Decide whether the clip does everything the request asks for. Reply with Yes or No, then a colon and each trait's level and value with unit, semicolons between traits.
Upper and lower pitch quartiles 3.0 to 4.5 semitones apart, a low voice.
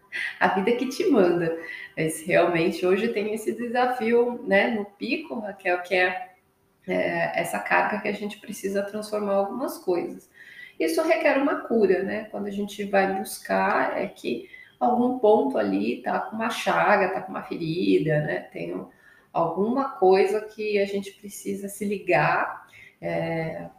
No: average, 4.2 semitones; high, 205 Hz